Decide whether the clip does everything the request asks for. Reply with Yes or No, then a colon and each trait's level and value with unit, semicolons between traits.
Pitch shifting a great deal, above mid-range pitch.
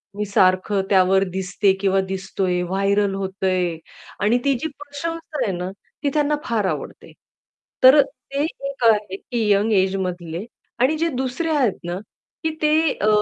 Yes: wide, 6.3 semitones; high, 200 Hz